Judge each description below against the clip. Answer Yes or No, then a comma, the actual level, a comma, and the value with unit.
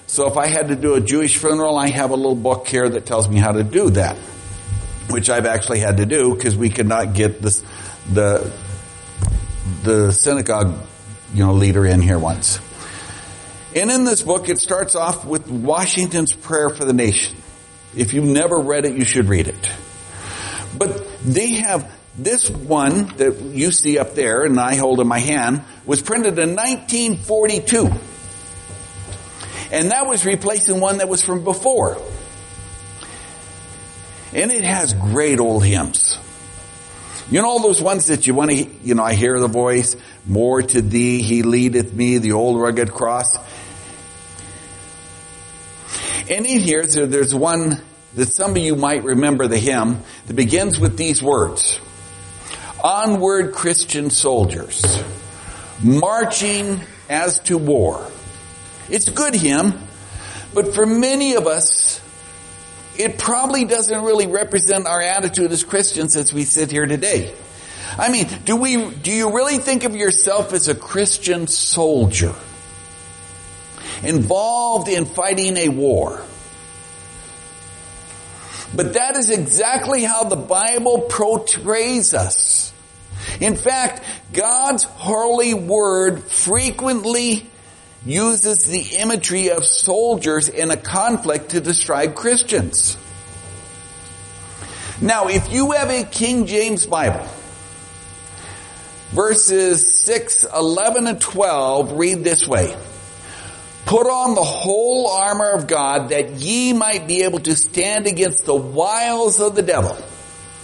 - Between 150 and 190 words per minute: No, average, 140 wpm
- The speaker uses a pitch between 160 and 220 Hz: No, low, 135 Hz